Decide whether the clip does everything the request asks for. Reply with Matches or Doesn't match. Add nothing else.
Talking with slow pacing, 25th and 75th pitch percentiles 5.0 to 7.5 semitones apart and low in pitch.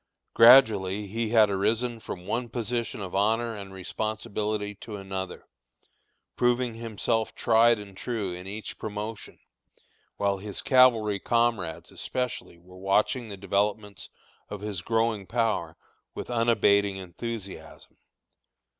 Doesn't match